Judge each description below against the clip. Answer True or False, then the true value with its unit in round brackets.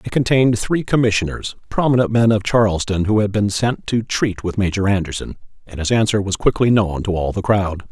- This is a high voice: False (105 Hz)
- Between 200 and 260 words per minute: True (205 wpm)